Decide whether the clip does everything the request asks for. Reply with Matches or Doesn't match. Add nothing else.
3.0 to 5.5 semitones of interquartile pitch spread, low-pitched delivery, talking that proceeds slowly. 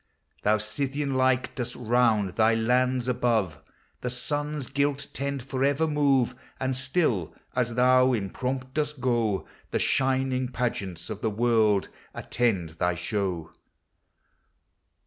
Matches